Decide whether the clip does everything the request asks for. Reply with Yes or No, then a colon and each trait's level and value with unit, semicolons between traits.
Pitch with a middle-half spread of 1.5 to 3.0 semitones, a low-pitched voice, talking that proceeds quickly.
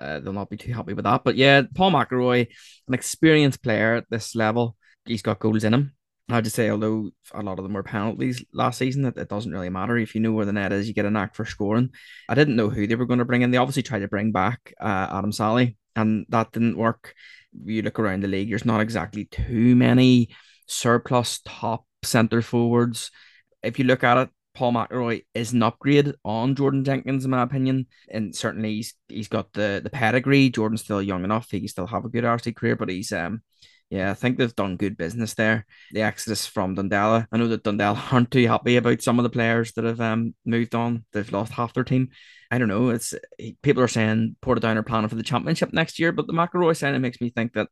Yes: narrow, 2.6 semitones; low, 115 Hz; fast, 235 wpm